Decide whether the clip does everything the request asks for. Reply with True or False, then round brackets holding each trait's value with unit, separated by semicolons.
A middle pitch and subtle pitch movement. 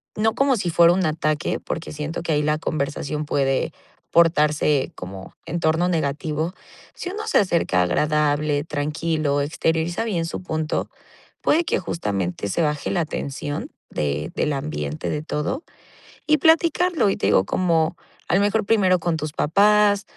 False (160 Hz; 3.9 semitones)